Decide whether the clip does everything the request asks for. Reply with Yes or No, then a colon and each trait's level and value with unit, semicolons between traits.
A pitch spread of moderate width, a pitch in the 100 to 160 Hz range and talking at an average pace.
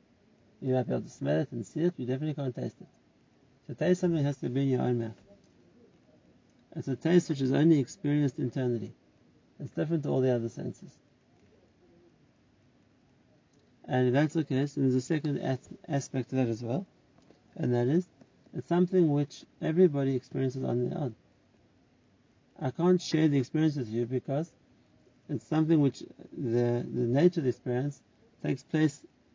Yes: average, 4.0 semitones; low, 135 Hz; average, 170 wpm